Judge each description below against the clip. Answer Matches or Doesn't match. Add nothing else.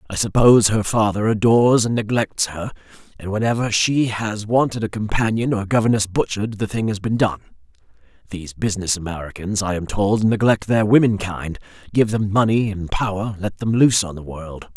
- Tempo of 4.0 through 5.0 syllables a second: Doesn't match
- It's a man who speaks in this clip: Matches